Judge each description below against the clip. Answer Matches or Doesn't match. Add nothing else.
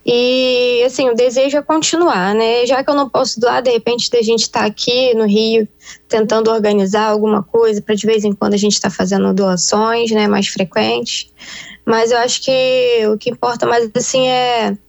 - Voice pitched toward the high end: Matches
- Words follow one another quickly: Matches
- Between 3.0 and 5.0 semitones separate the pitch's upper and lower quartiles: Doesn't match